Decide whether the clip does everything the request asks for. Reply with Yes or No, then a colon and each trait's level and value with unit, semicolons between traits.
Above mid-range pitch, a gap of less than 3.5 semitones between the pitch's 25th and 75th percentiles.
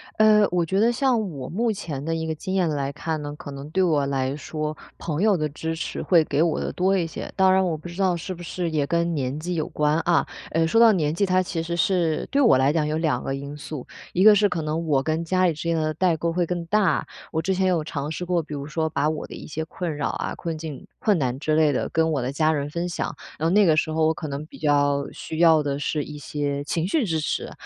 No: medium, 160 Hz; average, 3.1 semitones